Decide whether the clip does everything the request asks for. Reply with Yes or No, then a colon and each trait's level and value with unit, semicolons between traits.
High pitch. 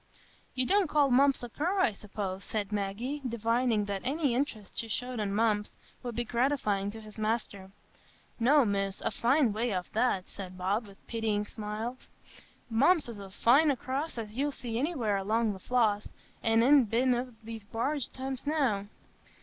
Yes: high, 230 Hz